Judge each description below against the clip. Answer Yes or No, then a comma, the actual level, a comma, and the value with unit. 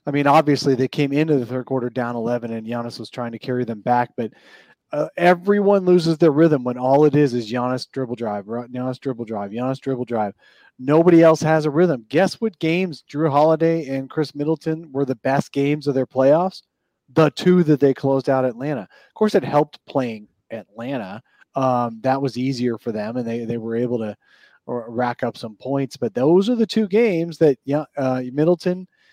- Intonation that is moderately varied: Yes, average, 4.6 semitones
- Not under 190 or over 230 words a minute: Yes, average, 200 wpm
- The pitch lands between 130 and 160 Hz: Yes, low, 135 Hz